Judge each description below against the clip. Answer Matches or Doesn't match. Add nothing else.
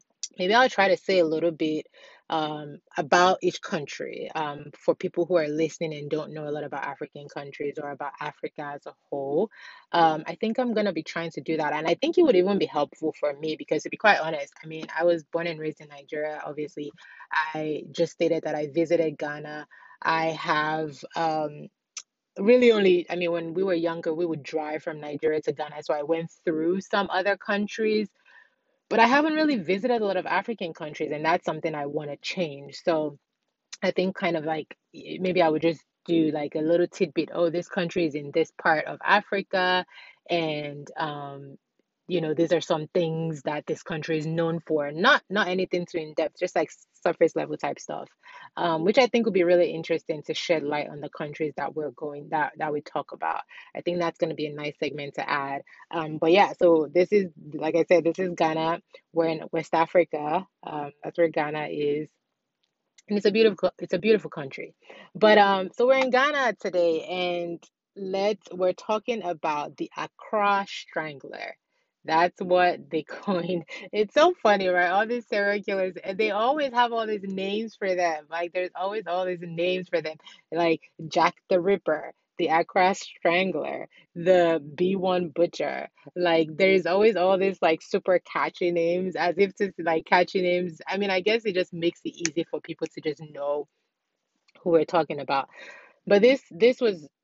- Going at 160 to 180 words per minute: Doesn't match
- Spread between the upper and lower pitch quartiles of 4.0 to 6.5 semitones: Doesn't match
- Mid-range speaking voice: Matches